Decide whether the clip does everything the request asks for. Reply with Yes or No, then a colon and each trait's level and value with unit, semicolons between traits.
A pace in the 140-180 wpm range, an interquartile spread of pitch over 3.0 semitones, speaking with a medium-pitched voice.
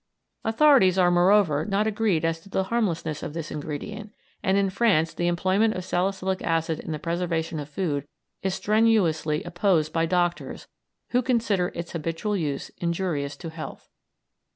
Yes: average, 155 wpm; average, 3.6 semitones; medium, 175 Hz